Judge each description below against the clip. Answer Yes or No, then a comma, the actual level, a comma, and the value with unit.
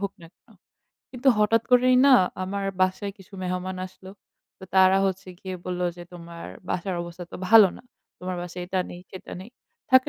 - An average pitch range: No, narrow, 2.0 semitones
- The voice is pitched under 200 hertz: Yes, high, 190 Hz